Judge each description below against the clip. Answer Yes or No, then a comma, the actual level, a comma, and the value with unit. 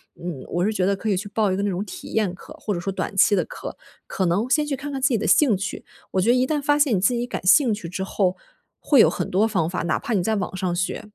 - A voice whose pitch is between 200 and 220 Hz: Yes, high, 205 Hz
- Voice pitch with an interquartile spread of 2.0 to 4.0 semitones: No, average, 4.7 semitones